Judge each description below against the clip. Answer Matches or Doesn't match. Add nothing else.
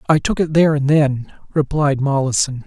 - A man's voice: Matches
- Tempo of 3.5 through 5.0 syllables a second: Doesn't match